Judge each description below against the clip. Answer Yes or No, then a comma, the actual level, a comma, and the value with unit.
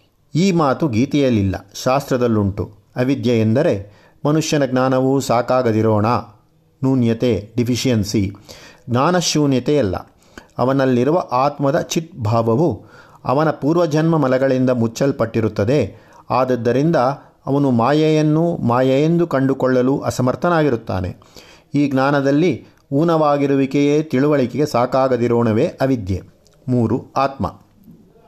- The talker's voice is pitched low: Yes, low, 130 Hz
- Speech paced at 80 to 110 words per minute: No, average, 70 wpm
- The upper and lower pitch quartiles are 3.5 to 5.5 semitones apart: Yes, average, 4.2 semitones